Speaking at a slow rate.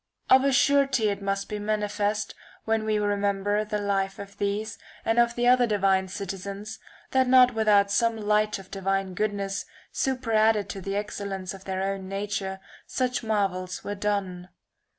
No: average, 170 wpm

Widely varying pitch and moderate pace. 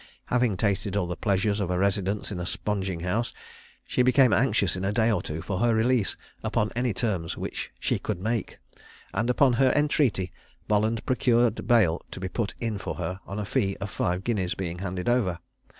No: average, 4.0 semitones; average, 195 wpm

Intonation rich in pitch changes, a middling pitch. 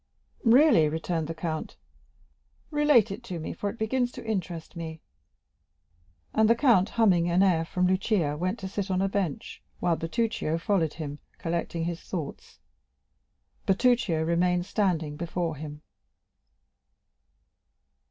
No: average, 3.9 semitones; medium, 180 Hz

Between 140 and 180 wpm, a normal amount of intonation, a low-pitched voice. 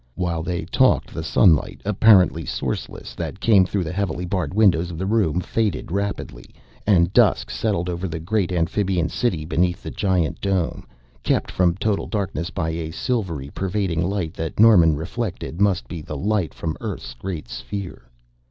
Yes: average, 165 wpm; average, 3.5 semitones; very low, 90 Hz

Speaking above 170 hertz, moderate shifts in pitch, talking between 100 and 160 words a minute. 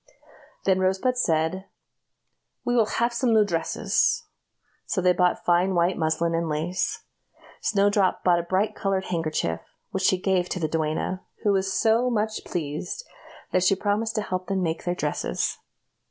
Yes: medium, 185 Hz; average, 3.2 semitones; average, 155 wpm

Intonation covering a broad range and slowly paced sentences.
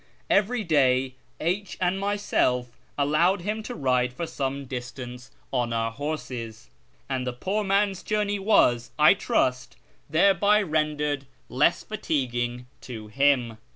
Yes: wide, 7.5 semitones; slow, 125 wpm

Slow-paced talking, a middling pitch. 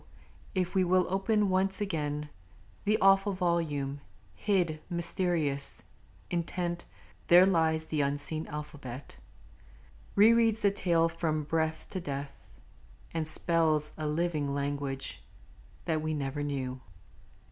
Yes: slow, 115 wpm; medium, 160 Hz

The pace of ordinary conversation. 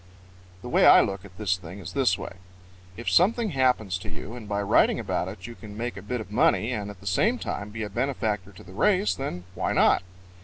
No: fast, 240 wpm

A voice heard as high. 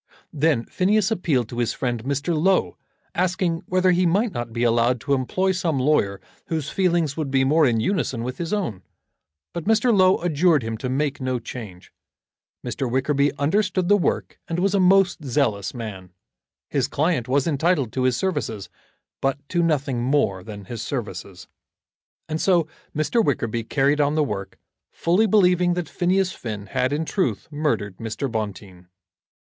No: medium, 145 Hz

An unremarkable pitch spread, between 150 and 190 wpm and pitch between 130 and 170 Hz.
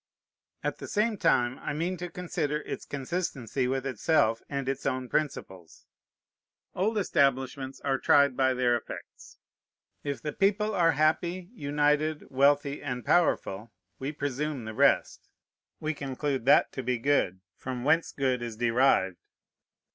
No: average, 3.5 semitones; average, 140 wpm; medium, 140 Hz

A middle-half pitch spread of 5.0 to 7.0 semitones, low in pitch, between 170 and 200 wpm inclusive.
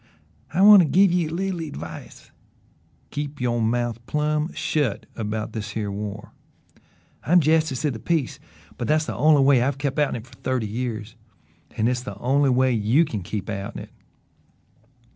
Yes: wide, 5.5 semitones; low, 130 Hz; average, 180 wpm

